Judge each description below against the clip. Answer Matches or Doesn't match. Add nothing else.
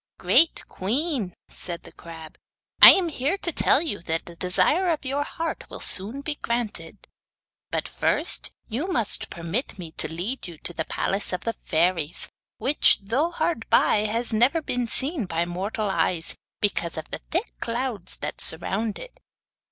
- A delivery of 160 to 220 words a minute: Matches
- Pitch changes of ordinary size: Doesn't match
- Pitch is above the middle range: Matches